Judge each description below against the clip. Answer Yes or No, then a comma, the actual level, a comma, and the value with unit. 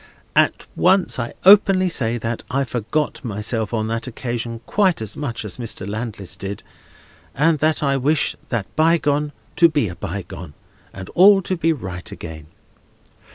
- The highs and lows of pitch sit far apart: Yes, wide, 6.6 semitones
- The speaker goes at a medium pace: Yes, average, 155 wpm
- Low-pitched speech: Yes, low, 120 Hz